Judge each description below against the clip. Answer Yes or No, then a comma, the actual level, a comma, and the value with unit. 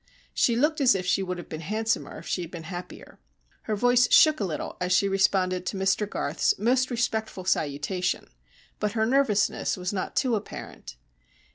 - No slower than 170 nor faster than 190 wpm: Yes, average, 180 wpm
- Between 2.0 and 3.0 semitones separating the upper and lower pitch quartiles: No, average, 4.3 semitones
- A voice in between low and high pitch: No, high, 195 Hz